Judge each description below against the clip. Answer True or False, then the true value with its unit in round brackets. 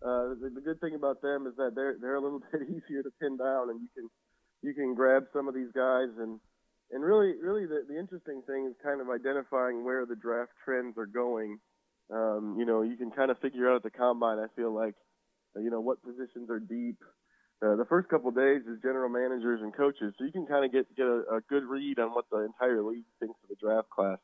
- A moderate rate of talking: False (245 wpm)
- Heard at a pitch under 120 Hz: False (125 Hz)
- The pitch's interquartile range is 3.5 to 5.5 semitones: False (2.8 semitones)